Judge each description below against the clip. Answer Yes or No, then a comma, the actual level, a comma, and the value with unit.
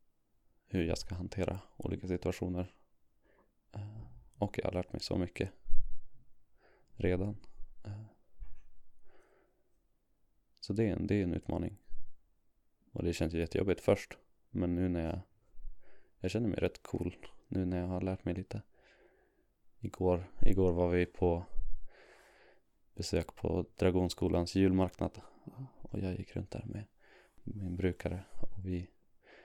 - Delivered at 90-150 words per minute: Yes, average, 130 wpm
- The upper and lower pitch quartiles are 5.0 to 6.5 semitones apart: No, narrow, 2.6 semitones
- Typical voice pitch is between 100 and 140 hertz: No, very low, 90 Hz